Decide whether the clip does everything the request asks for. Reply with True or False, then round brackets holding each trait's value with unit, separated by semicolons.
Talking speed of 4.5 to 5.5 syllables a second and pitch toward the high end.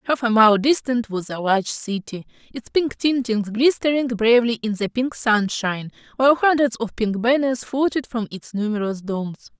True (5.0 syllables/s; 230 Hz)